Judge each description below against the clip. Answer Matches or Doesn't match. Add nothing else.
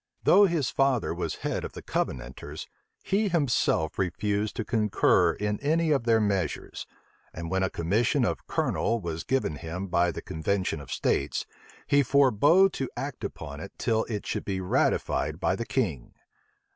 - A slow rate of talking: Doesn't match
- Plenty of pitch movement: Matches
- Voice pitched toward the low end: Matches